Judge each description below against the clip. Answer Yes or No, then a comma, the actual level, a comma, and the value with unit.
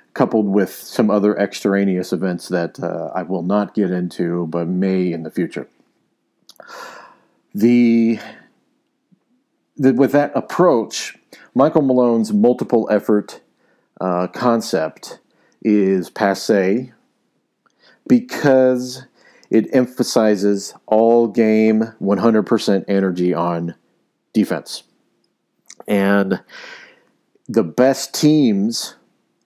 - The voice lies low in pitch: Yes, low, 110 Hz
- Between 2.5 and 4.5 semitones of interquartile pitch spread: No, average, 4.9 semitones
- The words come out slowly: Yes, slow, 90 wpm